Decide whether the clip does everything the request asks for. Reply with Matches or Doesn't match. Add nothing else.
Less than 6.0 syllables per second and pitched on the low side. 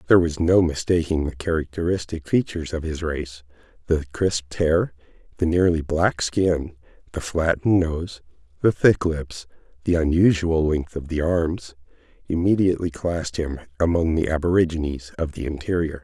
Matches